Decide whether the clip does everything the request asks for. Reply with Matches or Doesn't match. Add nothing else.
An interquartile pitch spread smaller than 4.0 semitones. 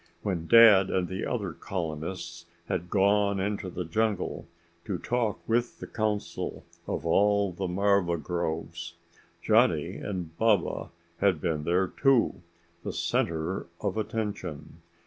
Matches